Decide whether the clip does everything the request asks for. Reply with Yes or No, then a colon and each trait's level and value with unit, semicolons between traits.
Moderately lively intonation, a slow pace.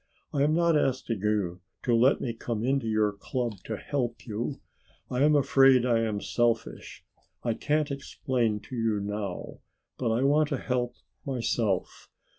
No: average, 3.7 semitones; average, 165 wpm